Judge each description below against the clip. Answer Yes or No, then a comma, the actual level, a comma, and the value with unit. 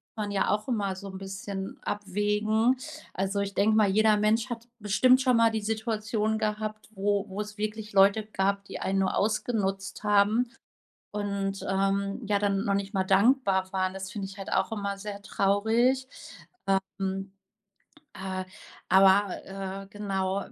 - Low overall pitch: No, high, 205 Hz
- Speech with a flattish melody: Yes, narrow, 1.8 semitones